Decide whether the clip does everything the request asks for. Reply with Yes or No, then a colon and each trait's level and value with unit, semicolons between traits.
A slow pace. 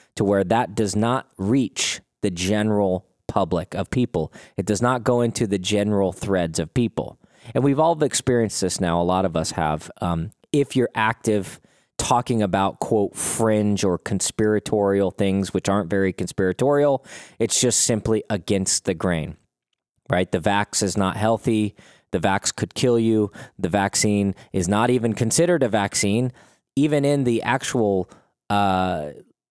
No: average, 155 wpm